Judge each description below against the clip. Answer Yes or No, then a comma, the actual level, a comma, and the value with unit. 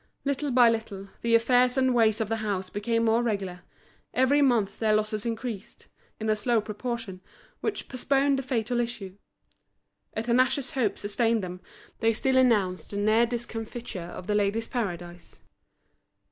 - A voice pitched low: No, high, 225 Hz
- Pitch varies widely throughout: No, average, 3.0 semitones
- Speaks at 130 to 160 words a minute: Yes, average, 155 wpm